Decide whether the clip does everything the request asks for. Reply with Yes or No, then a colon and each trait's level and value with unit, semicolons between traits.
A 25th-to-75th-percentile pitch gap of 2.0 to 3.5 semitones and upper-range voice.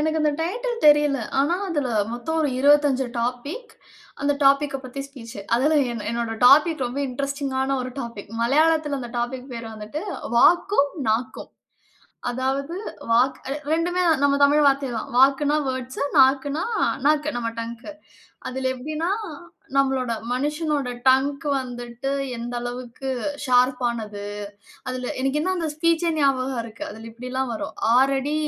Yes: average, 3.0 semitones; very high, 270 Hz